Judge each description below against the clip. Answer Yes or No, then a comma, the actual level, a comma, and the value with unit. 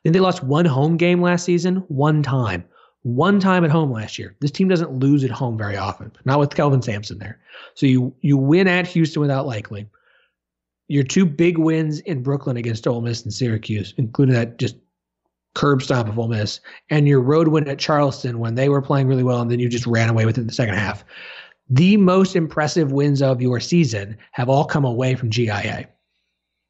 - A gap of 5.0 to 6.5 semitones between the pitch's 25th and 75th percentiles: Yes, average, 5.3 semitones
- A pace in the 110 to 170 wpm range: No, fast, 205 wpm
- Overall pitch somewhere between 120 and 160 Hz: Yes, low, 135 Hz